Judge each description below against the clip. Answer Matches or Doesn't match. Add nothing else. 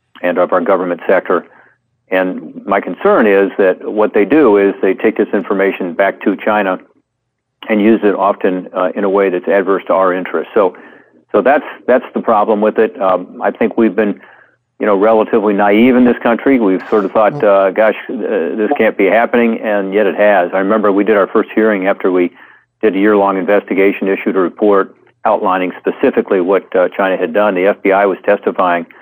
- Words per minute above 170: Matches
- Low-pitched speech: Matches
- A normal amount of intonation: Doesn't match